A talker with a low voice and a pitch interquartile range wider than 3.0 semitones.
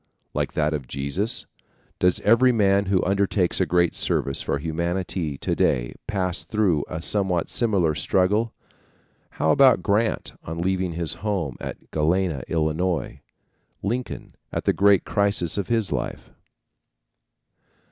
Yes: very low, 90 Hz; average, 4.2 semitones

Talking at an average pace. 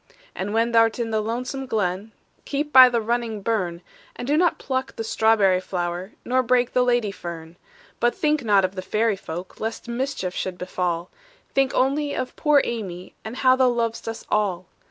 Yes: average, 190 wpm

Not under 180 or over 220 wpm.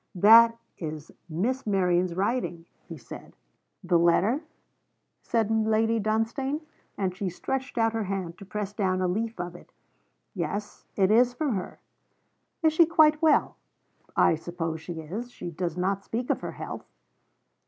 No: average, 155 wpm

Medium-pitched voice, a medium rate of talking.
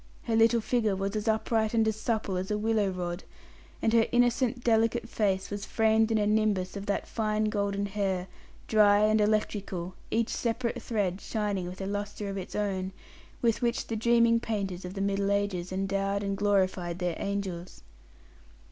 No: high, 205 Hz; average, 175 wpm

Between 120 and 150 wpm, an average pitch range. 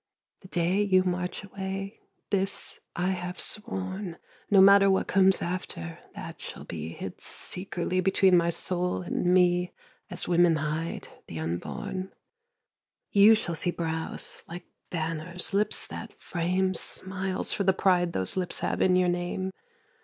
No: average, 145 wpm; narrow, 1.8 semitones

